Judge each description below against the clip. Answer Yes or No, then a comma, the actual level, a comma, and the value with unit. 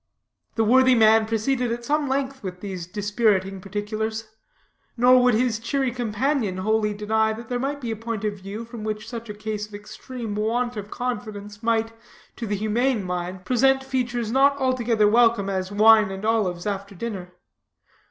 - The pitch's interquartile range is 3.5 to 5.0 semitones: No, average, 2.9 semitones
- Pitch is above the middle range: Yes, high, 220 Hz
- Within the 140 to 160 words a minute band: No, average, 170 wpm